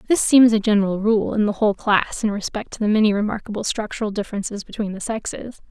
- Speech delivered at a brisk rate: Yes, fast, 210 wpm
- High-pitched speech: Yes, high, 210 Hz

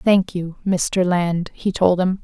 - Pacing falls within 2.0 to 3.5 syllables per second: Yes, 3.4 syllables/s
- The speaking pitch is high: No, medium, 180 Hz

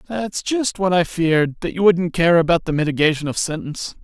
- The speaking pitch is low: No, medium, 170 Hz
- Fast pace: Yes, fast, 210 wpm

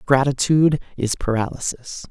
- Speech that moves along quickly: No, slow, 85 wpm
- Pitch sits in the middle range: No, low, 130 Hz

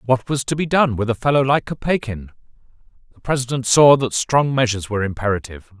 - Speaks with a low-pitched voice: Yes, low, 125 Hz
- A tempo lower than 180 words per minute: No, average, 185 wpm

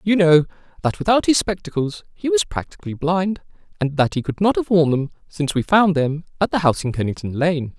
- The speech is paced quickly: Yes, fast, 215 wpm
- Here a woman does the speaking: No, male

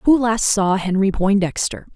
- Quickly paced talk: No, average, 155 wpm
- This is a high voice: Yes, high, 205 Hz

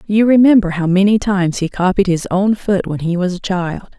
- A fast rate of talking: Yes, fast, 225 wpm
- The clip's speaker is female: Yes, female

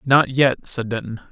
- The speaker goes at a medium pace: Yes, average, 185 wpm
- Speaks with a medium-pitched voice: No, low, 125 Hz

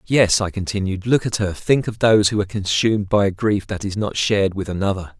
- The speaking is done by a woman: No, male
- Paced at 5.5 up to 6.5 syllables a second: Yes, 5.9 syllables/s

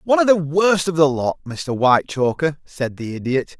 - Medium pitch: Yes, medium, 150 Hz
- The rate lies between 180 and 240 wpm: Yes, average, 200 wpm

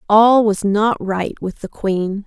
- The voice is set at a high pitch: Yes, high, 205 Hz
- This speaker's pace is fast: No, average, 185 wpm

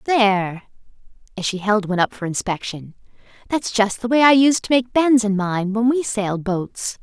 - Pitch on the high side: Yes, high, 215 Hz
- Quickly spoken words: No, average, 195 wpm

